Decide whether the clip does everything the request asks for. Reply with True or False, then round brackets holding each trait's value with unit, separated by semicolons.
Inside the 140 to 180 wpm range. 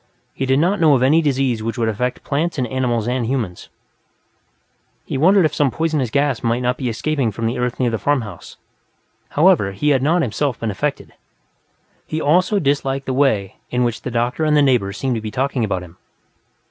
False (200 wpm)